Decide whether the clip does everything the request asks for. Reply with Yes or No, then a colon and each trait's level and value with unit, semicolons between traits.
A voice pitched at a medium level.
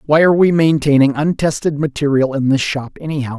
Yes: medium, 145 Hz